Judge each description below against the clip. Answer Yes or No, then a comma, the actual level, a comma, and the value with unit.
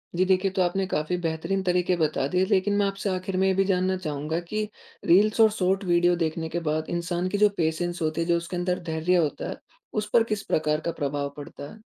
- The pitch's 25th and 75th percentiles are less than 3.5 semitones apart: Yes, average, 2.9 semitones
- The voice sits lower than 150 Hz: No, medium, 180 Hz